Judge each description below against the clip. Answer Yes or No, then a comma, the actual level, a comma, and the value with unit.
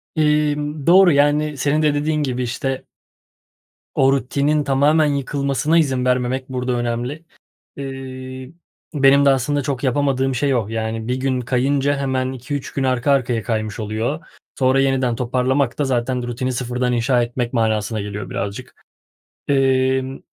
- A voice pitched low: Yes, low, 130 Hz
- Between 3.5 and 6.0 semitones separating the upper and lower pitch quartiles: No, narrow, 2.4 semitones